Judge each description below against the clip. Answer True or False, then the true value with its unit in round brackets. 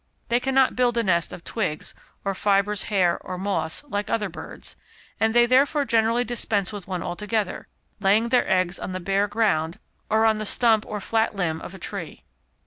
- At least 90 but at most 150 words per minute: False (190 wpm)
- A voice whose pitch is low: False (210 Hz)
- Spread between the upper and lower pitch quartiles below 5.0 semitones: True (3.6 semitones)